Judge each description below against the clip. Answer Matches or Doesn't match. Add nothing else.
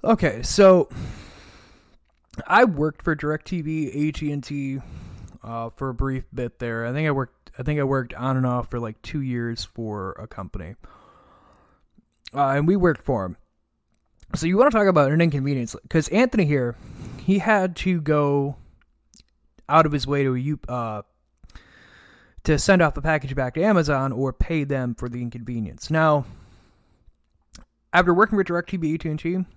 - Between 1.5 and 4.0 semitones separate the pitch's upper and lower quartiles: Doesn't match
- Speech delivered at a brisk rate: Doesn't match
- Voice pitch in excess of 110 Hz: Matches